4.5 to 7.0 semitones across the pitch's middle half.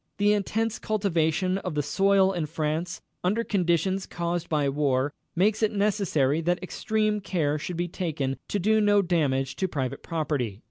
Yes: average, 4.8 semitones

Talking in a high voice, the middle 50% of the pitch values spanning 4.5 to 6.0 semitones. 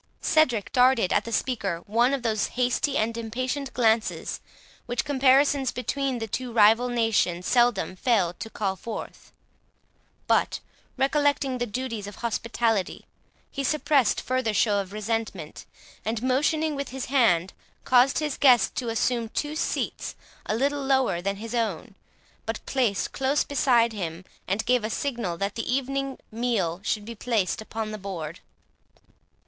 No: high, 235 Hz; average, 3.8 semitones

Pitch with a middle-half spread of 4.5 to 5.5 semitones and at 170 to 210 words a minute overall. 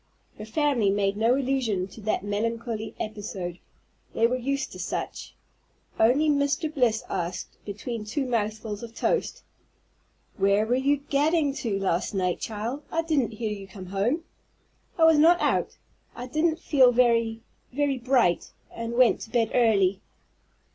No: average, 4.9 semitones; average, 150 wpm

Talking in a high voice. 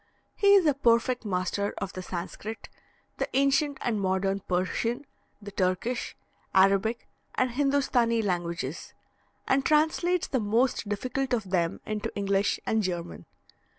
Yes: high, 220 Hz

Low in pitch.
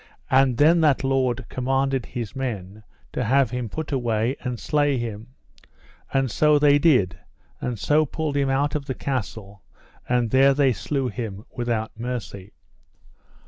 Yes: low, 130 Hz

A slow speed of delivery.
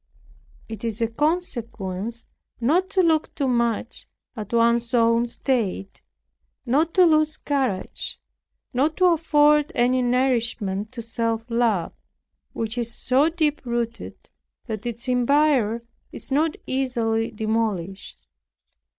Yes: slow, 115 wpm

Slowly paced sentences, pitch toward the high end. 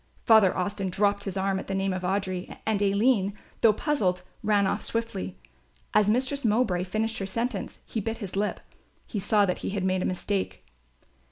No: average, 185 wpm; high, 200 Hz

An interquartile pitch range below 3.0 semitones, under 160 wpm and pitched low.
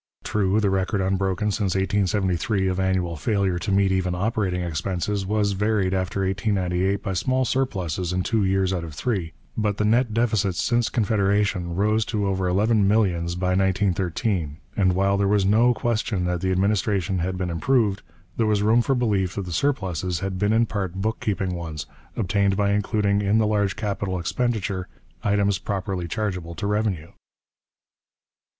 No: narrow, 2.4 semitones; average, 170 wpm; low, 100 Hz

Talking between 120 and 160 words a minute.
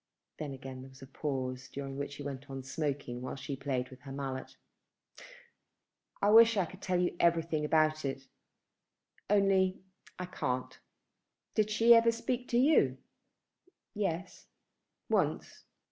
Yes: average, 145 wpm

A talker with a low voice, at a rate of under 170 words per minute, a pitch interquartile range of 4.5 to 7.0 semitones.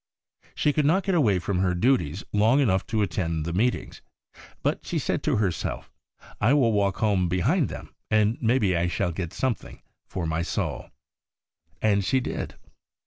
No: low, 105 Hz; average, 180 wpm; average, 5.3 semitones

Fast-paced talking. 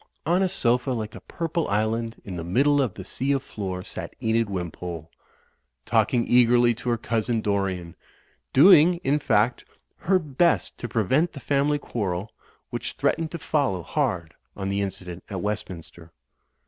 No: average, 165 wpm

